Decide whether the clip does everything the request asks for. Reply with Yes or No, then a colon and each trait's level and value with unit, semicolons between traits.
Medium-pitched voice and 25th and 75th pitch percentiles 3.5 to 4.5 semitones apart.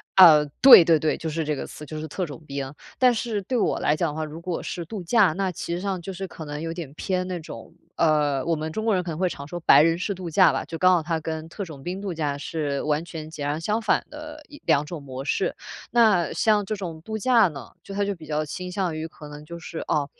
Yes: medium, 165 Hz; average, 3.9 semitones